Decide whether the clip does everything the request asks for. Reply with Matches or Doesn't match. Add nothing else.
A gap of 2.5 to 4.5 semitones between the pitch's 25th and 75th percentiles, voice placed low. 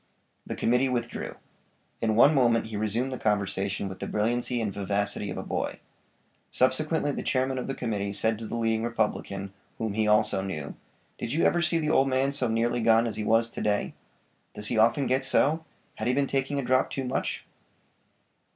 Matches